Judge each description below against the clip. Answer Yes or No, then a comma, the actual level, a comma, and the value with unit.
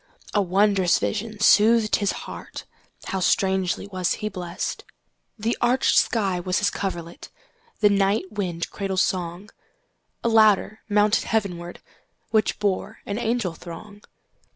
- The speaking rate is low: Yes, slow, 105 wpm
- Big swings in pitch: No, average, 2.7 semitones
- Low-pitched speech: No, high, 200 Hz